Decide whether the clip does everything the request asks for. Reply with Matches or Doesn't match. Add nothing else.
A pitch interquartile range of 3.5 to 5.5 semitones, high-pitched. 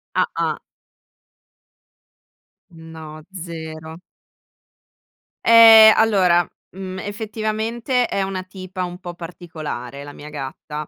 Doesn't match